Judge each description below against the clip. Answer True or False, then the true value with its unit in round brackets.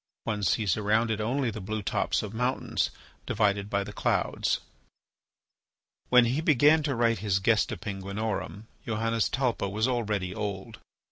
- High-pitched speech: False (110 Hz)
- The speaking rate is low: False (145 wpm)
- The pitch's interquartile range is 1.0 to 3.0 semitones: True (2.7 semitones)